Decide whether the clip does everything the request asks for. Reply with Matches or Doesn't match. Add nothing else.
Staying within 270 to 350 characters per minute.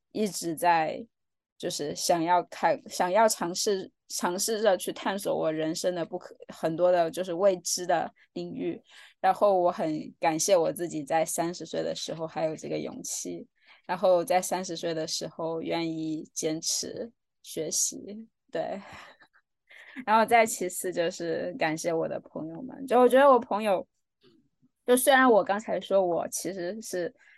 Doesn't match